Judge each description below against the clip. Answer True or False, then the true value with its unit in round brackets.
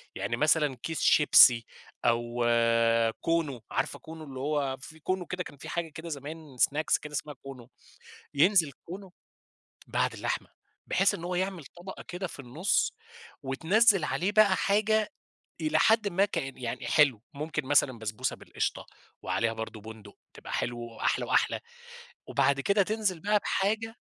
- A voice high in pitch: False (155 Hz)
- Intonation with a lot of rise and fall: True (6.2 semitones)